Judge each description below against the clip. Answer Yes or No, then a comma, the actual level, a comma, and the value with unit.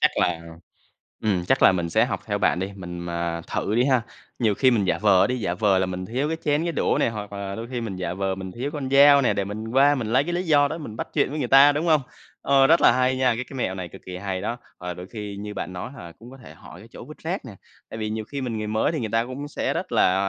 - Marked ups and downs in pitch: Yes, wide, 6.0 semitones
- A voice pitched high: No, low, 110 Hz